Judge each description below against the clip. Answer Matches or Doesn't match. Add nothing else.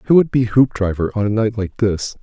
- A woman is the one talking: Doesn't match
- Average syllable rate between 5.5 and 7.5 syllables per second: Matches